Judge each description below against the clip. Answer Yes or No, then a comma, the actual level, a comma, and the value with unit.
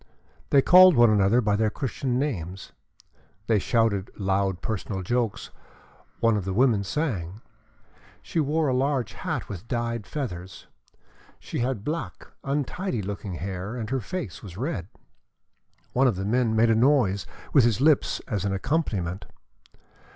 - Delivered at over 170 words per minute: No, average, 150 wpm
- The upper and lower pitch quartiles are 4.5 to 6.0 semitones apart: Yes, average, 5.3 semitones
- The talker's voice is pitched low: Yes, low, 115 Hz